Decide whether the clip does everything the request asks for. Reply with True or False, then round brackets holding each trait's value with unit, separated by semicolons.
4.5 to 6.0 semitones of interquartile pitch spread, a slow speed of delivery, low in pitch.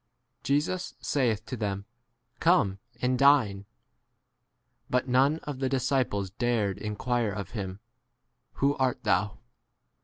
True (5.0 semitones; 120 wpm; 120 Hz)